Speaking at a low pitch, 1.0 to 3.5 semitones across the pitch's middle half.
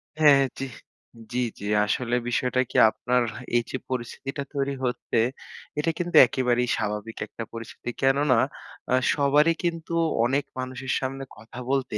Yes: low, 130 Hz; narrow, 2.5 semitones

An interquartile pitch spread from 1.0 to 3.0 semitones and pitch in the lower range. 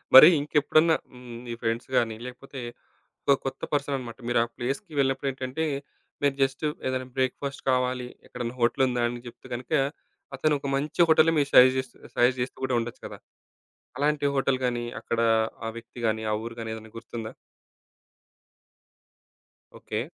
Yes: narrow, 2.5 semitones; low, 130 Hz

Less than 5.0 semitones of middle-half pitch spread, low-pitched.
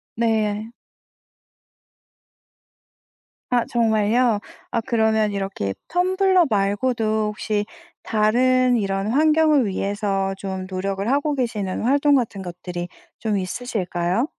No: average, 4.2 semitones; high, 220 Hz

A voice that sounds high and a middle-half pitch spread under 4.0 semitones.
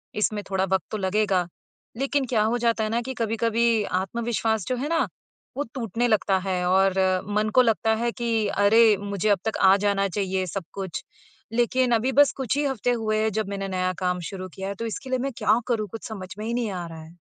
Yes: high, 215 Hz; average, 3.4 semitones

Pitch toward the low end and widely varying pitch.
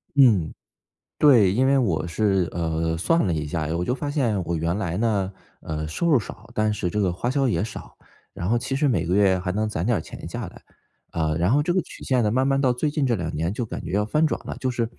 Yes: low, 105 Hz; wide, 6.9 semitones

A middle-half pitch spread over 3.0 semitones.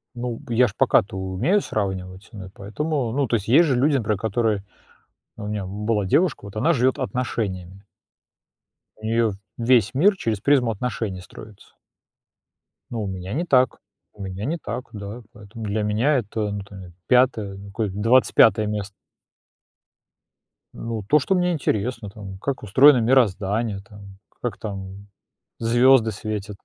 Yes: average, 3.9 semitones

